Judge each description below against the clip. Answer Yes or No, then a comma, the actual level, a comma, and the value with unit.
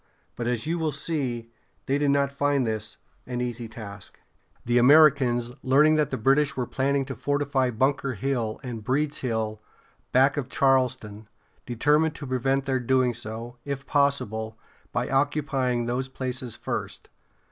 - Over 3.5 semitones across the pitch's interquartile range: No, average, 2.8 semitones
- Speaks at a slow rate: No, average, 150 wpm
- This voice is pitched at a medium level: No, low, 130 Hz